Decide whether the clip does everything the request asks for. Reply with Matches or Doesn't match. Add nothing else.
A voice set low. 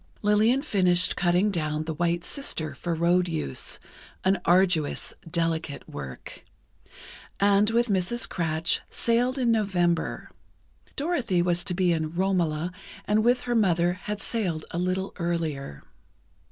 Doesn't match